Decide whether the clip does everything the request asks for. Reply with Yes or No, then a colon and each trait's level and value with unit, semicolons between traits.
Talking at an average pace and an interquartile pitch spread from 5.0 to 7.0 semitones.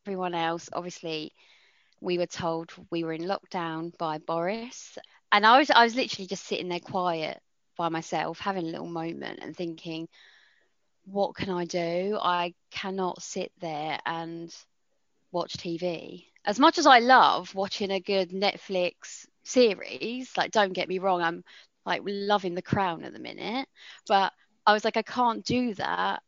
No: average, 165 wpm; average, 3.5 semitones